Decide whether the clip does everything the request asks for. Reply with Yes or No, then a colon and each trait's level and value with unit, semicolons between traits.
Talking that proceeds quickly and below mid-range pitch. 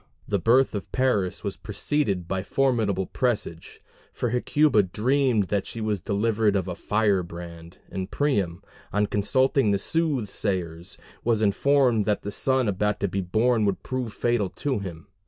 No: average, 155 wpm; low, 105 Hz